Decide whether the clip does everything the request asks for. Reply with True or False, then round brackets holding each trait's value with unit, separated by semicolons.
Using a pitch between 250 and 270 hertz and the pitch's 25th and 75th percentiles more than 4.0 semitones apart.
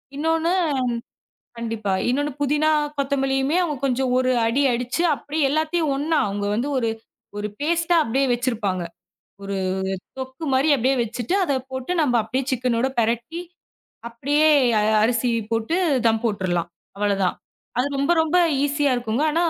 True (260 Hz; 4.4 semitones)